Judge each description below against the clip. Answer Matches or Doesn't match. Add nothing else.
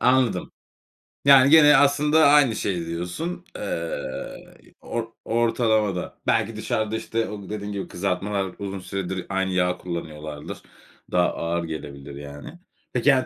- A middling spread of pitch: Doesn't match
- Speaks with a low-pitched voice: Matches